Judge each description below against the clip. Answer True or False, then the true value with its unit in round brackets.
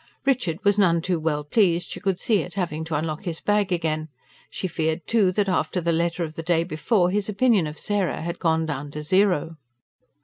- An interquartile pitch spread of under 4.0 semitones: True (3.5 semitones)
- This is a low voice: False (170 Hz)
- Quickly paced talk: True (210 wpm)